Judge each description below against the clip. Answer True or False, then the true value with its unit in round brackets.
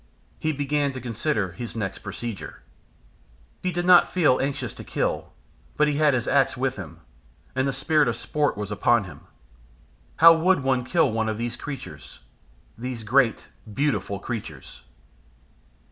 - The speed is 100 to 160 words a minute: True (155 wpm)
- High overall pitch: False (130 Hz)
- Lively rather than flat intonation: False (4.8 semitones)